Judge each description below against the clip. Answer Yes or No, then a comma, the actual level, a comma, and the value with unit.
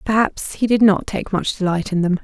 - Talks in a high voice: Yes, high, 200 Hz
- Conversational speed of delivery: No, fast, 240 wpm